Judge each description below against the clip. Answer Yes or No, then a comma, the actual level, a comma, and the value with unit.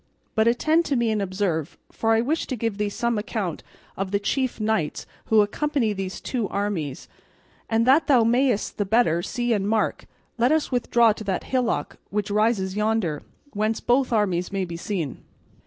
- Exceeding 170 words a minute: Yes, average, 180 wpm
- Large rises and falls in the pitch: No, average, 3.4 semitones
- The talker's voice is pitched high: Yes, high, 215 Hz